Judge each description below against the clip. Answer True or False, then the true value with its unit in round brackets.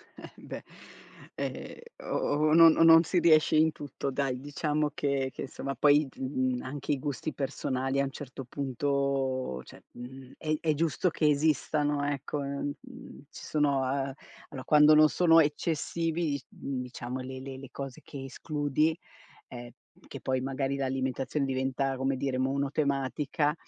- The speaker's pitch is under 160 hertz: True (140 Hz)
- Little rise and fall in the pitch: True (2.2 semitones)